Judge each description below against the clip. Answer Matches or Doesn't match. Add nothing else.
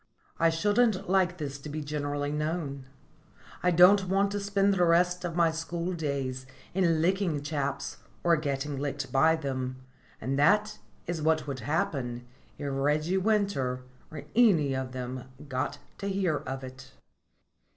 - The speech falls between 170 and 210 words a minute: Doesn't match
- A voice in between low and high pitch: Matches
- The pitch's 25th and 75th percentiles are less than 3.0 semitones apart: Doesn't match